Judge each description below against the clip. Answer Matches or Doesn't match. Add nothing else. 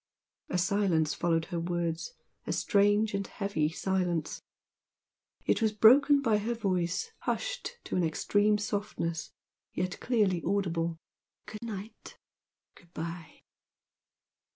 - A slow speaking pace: Matches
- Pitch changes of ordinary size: Matches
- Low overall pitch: Doesn't match